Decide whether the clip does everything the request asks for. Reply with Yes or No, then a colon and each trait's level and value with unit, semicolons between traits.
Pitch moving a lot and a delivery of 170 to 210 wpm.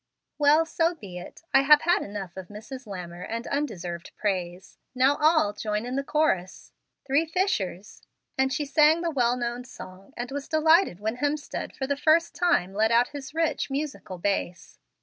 Yes: wide, 7.1 semitones; average, 180 wpm